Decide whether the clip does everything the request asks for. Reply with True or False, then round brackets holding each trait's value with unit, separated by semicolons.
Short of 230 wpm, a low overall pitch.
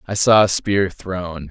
True (200 wpm; 95 Hz)